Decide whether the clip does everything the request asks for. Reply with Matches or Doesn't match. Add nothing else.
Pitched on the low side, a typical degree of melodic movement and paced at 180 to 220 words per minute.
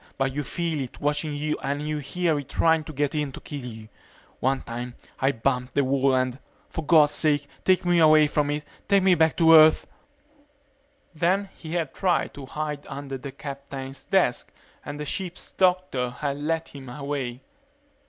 Doesn't match